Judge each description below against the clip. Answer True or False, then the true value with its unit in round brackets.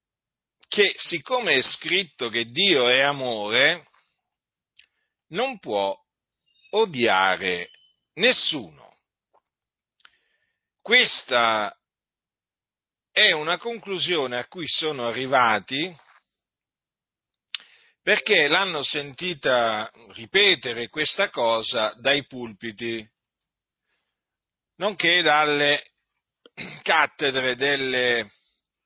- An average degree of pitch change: False (7.1 semitones)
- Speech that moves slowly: True (65 wpm)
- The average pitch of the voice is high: False (140 Hz)